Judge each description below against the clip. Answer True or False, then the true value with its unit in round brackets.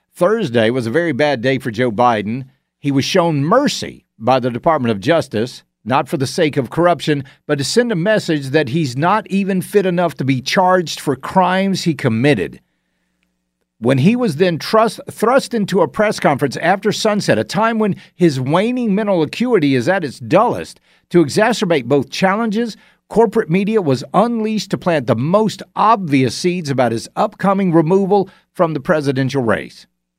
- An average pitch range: False (6.9 semitones)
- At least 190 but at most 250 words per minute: False (175 wpm)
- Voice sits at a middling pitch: True (170 Hz)